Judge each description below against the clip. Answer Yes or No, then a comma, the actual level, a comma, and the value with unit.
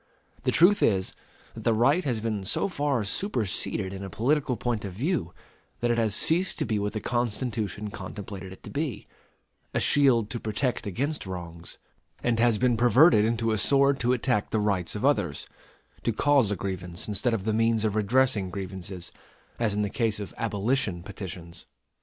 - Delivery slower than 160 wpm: No, average, 185 wpm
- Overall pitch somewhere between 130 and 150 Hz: No, low, 110 Hz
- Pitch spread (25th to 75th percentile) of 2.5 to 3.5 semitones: No, average, 3.9 semitones